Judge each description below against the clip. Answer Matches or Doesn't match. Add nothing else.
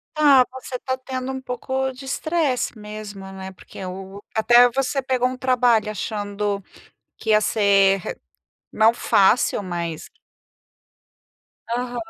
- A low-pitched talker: Doesn't match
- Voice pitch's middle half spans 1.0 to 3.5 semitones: Doesn't match